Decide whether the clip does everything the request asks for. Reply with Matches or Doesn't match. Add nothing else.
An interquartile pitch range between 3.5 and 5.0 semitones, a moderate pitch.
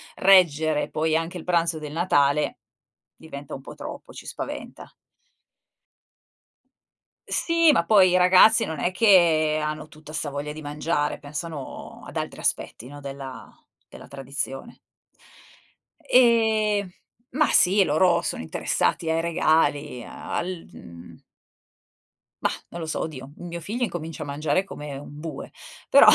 Matches